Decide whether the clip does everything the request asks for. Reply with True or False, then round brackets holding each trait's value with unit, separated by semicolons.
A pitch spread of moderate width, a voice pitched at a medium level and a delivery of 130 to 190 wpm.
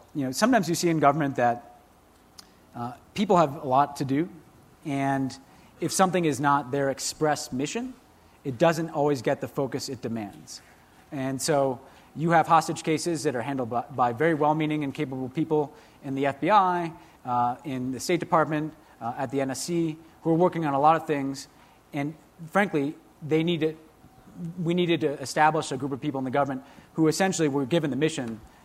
True (3.2 semitones; 145 Hz; 180 wpm)